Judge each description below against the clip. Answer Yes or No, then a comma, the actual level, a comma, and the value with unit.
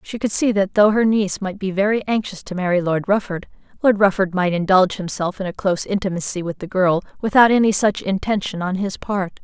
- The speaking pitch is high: Yes, high, 195 Hz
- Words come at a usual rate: No, fast, 215 wpm